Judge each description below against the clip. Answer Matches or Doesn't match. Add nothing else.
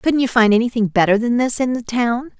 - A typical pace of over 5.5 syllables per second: Matches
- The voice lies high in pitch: Matches